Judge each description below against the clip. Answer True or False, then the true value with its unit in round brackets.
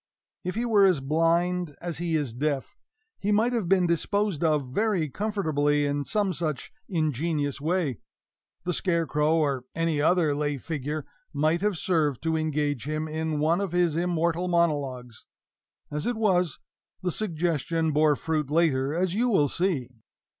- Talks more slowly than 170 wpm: True (155 wpm)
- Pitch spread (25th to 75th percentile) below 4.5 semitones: True (3.4 semitones)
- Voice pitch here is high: False (160 Hz)